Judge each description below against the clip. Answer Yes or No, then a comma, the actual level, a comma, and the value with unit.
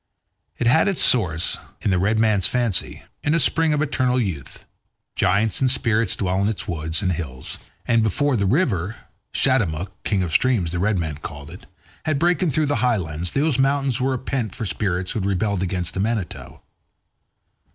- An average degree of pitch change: No, wide, 6.3 semitones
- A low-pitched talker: Yes, low, 105 Hz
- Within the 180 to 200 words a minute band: Yes, average, 185 wpm